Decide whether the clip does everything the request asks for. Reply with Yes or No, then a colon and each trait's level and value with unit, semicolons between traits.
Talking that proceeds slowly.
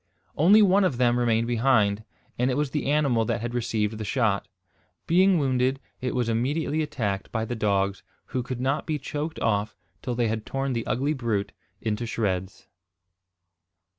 No: average, 170 wpm